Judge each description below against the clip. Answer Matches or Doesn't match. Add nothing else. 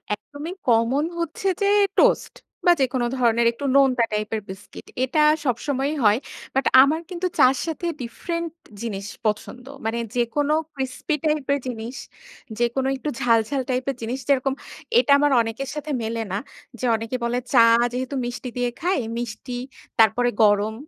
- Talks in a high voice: Matches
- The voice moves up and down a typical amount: Matches